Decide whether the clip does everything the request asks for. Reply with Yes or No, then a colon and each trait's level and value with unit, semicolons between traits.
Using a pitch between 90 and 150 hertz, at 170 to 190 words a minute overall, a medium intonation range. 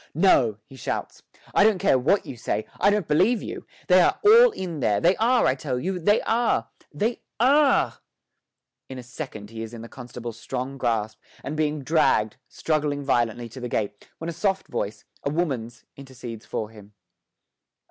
No: low, 135 Hz; average, 180 wpm; wide, 7.7 semitones